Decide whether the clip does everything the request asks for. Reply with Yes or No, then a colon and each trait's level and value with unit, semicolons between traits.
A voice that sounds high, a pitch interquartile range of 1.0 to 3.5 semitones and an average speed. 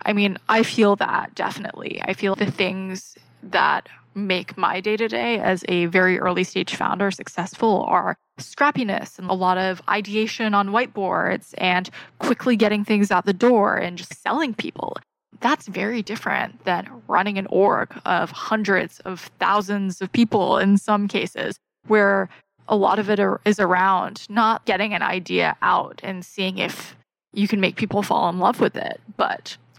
Yes: high, 200 Hz; narrow, 2.5 semitones; average, 165 wpm